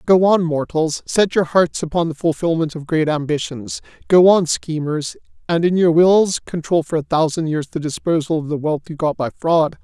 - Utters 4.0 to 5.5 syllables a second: Yes, 4.9 syllables/s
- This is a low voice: No, medium, 160 Hz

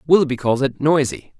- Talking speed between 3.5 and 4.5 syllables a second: No, 5.7 syllables/s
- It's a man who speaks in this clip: Yes, male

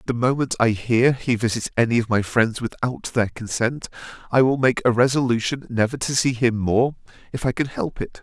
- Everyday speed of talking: No, fast, 210 wpm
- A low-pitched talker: Yes, low, 120 Hz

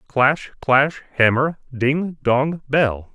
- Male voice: Yes, male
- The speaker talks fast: No, slow, 115 wpm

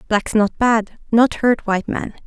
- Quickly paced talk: No, average, 185 wpm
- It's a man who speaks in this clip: No, female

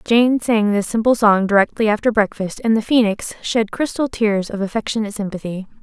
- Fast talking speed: No, average, 175 wpm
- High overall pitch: Yes, high, 215 Hz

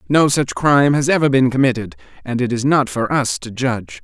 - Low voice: Yes, low, 125 Hz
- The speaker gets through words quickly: Yes, fast, 225 wpm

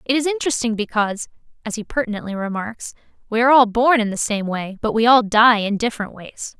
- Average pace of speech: No, fast, 210 wpm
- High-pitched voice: Yes, high, 225 Hz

